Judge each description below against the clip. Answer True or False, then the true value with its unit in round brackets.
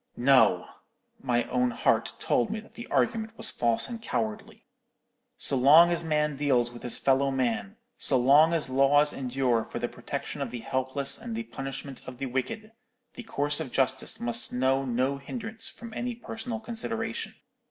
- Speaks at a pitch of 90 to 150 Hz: True (140 Hz)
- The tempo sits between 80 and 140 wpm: False (170 wpm)